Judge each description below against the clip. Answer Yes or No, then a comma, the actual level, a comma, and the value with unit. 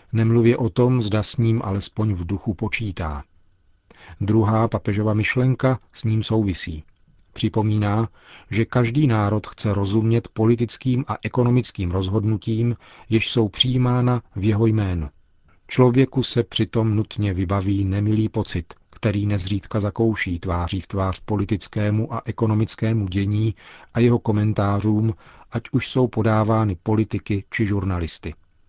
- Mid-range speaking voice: No, low, 110 Hz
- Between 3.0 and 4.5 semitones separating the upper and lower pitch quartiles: No, narrow, 2.4 semitones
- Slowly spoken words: No, average, 125 wpm